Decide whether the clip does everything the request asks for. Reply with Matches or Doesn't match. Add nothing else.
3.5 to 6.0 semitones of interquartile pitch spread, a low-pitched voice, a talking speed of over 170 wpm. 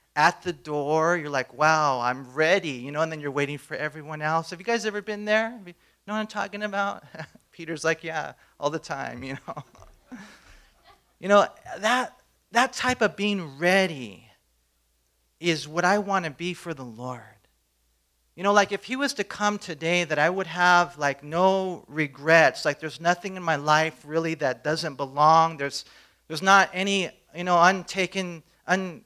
Doesn't match